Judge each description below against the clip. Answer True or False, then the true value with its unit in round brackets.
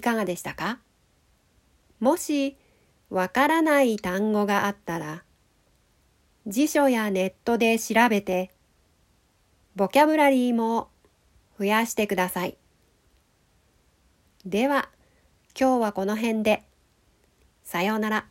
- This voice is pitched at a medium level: False (215 Hz)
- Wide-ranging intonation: False (4.8 semitones)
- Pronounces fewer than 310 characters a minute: True (205 characters per minute)